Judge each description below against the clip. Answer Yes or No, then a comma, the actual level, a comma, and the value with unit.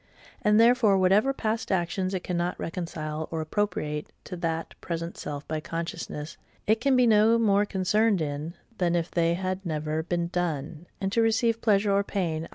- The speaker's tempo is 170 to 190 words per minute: Yes, average, 175 wpm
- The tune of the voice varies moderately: Yes, average, 4.3 semitones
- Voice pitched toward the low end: No, medium, 180 Hz